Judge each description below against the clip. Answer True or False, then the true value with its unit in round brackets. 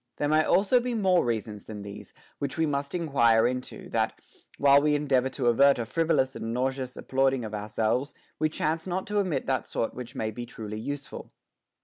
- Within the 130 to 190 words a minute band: False (200 wpm)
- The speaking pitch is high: False (135 Hz)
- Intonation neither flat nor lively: True (4.7 semitones)